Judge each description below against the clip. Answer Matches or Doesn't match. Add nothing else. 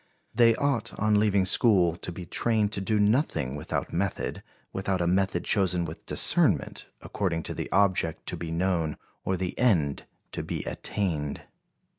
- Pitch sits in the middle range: Doesn't match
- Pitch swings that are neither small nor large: Matches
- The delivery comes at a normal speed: Matches